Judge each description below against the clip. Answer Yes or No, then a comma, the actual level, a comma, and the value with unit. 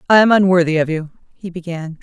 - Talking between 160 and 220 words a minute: Yes, fast, 205 wpm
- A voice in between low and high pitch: Yes, medium, 175 Hz